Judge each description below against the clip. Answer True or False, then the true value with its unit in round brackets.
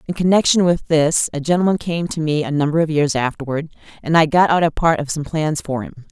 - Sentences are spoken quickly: True (245 wpm)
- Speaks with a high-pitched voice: False (155 Hz)